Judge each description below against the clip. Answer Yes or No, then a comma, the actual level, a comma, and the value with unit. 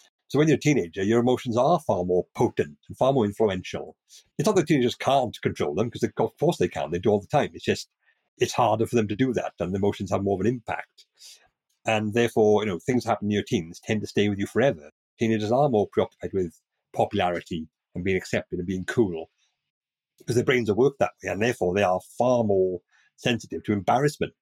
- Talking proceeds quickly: Yes, fast, 230 wpm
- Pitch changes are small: No, average, 4.1 semitones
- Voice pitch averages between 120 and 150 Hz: No, low, 105 Hz